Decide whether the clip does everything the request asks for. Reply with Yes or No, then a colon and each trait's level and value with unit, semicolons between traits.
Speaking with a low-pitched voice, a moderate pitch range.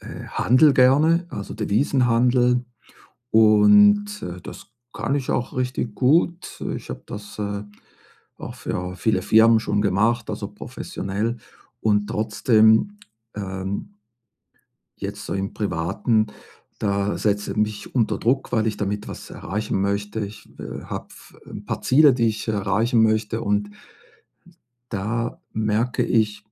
Yes: low, 110 Hz; average, 3.1 semitones